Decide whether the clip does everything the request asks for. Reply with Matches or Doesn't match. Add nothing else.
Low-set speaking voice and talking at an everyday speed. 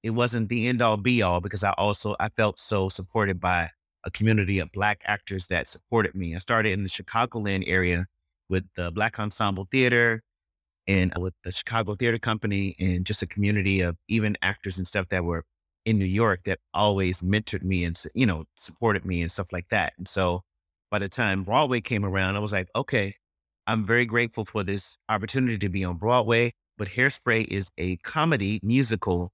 Matches